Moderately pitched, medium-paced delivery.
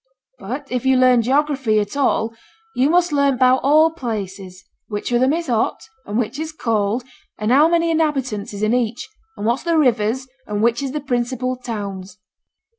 No: very high, 250 Hz; average, 185 wpm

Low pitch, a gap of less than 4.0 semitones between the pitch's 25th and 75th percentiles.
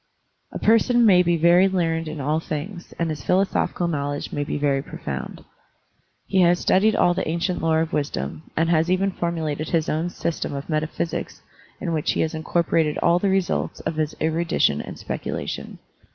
No: medium, 165 Hz; narrow, 2.5 semitones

